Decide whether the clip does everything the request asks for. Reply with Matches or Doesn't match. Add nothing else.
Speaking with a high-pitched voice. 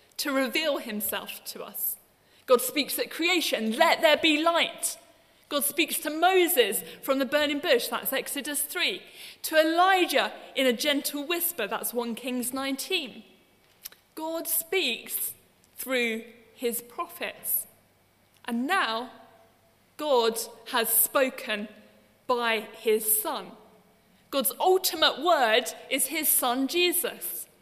Matches